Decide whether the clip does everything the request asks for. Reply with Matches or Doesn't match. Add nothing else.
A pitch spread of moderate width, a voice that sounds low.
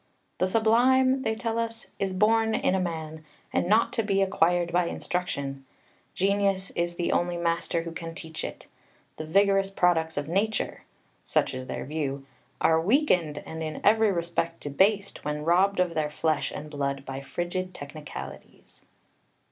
Doesn't match